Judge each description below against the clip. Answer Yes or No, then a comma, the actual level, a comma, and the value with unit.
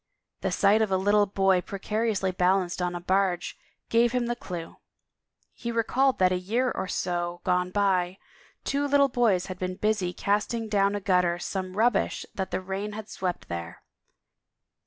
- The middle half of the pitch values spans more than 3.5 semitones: No, average, 3.1 semitones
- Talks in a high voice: Yes, high, 195 Hz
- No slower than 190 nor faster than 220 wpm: No, average, 170 wpm